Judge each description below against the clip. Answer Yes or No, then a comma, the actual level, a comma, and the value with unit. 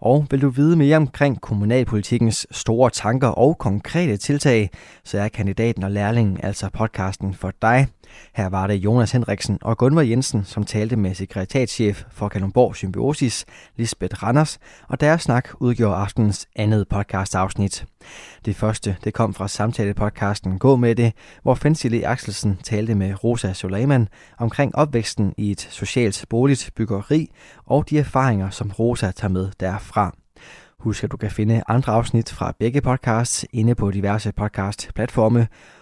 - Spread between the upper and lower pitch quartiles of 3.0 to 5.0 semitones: Yes, average, 3.6 semitones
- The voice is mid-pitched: No, low, 110 Hz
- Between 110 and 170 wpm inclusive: Yes, average, 150 wpm